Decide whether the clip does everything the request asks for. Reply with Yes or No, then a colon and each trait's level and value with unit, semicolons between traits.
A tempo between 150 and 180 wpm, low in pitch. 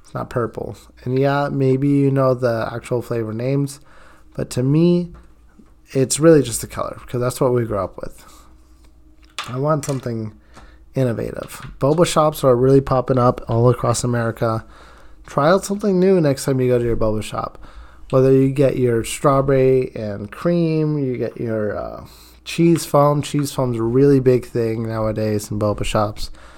Yes: average, 165 wpm; low, 125 Hz